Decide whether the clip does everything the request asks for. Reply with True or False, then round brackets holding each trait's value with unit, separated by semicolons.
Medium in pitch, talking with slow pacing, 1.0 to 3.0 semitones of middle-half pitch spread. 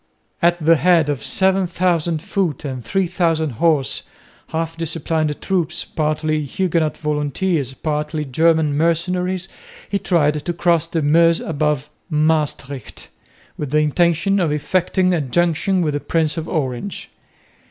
True (160 Hz; 130 wpm; 2.5 semitones)